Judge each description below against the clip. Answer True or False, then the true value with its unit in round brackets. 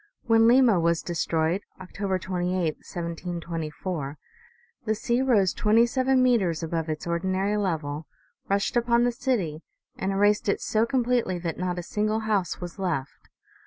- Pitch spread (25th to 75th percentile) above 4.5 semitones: True (5.0 semitones)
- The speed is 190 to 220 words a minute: False (145 wpm)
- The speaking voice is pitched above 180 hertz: True (190 Hz)